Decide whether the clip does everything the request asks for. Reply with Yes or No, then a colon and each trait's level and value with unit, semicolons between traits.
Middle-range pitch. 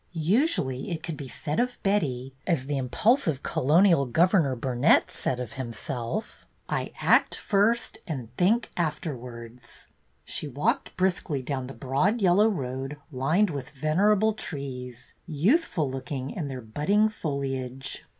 Yes: medium, 145 Hz